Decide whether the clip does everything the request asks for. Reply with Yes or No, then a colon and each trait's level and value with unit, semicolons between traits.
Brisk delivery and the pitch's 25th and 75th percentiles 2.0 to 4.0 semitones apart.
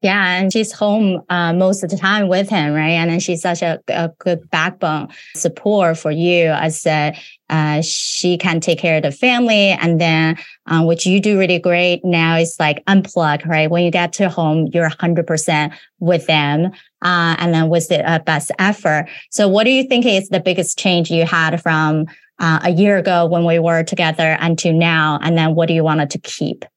Yes: fast, 210 wpm; narrow, 2.4 semitones